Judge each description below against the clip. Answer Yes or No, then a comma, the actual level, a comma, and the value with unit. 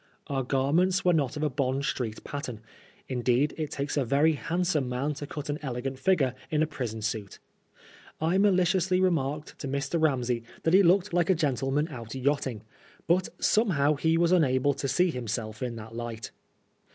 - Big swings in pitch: No, average, 4.6 semitones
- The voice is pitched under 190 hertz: Yes, medium, 140 Hz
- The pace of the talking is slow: No, average, 180 wpm